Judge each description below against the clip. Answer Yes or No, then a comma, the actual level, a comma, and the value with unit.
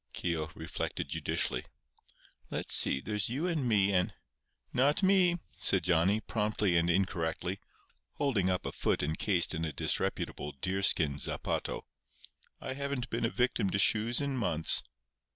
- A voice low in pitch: Yes, low, 100 Hz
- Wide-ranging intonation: Yes, wide, 6.5 semitones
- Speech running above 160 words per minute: No, slow, 135 wpm